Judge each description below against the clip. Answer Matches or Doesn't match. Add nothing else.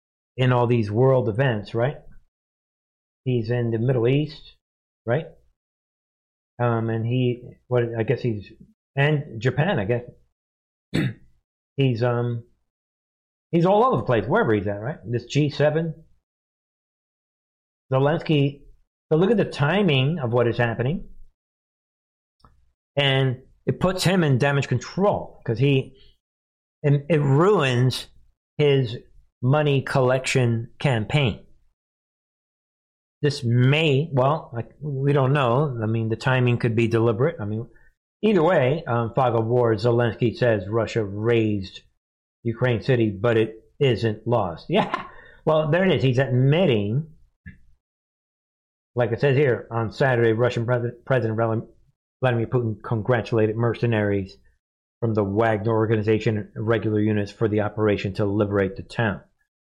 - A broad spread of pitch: Doesn't match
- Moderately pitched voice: Doesn't match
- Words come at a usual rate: Doesn't match